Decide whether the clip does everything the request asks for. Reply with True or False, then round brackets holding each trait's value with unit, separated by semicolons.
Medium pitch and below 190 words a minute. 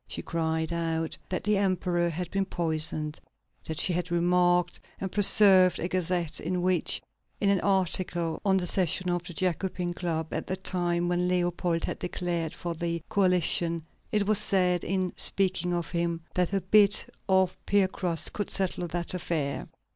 True (175 Hz; 165 wpm)